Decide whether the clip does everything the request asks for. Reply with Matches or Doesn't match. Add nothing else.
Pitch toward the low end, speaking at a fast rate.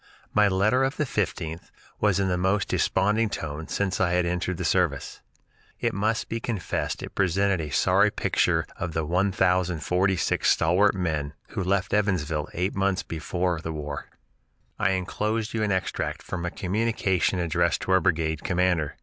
Doesn't match